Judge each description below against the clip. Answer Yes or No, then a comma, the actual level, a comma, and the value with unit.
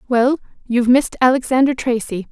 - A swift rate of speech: No, slow, 130 wpm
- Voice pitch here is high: Yes, very high, 250 Hz